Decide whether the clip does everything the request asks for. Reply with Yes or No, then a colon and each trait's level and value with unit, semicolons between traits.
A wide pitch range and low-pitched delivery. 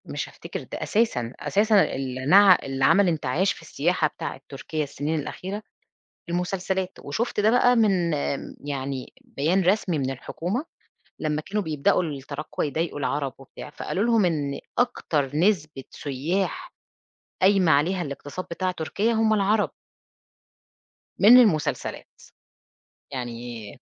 No: wide, 6.0 semitones; medium, 165 Hz